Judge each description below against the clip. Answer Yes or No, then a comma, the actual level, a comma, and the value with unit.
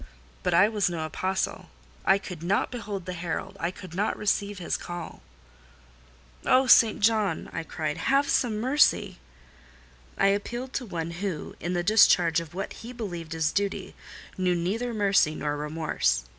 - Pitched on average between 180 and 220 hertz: Yes, medium, 185 Hz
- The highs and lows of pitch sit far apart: No, average, 4.2 semitones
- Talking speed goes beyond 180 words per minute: No, average, 155 wpm